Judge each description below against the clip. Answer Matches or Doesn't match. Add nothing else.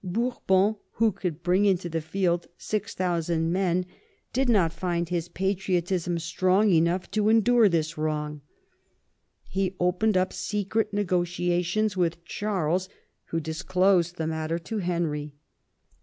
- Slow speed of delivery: Matches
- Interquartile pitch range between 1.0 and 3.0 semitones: Matches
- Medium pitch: Matches